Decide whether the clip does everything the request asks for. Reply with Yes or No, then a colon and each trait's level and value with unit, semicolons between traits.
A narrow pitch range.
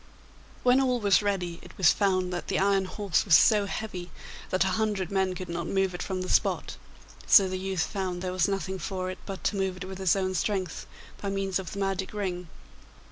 Yes: narrow, 1.4 semitones